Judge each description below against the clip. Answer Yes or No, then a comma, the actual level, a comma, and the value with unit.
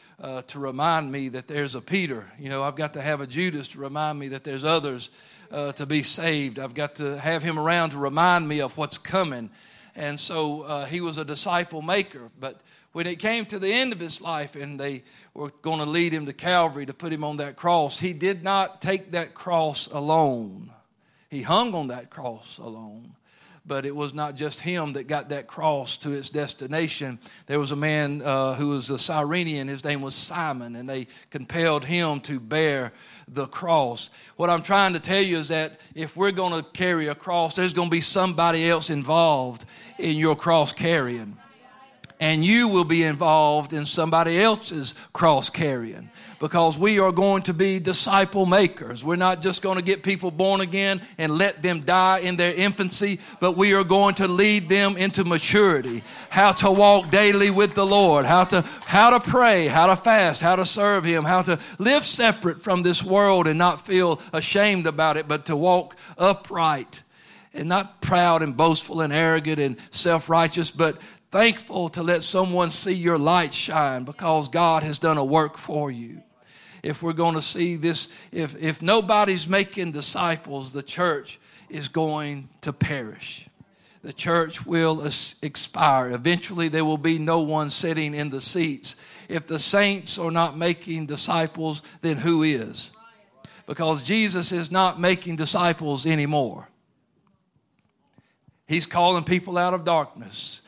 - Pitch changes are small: No, average, 3.7 semitones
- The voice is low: No, medium, 165 Hz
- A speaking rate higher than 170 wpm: Yes, average, 180 wpm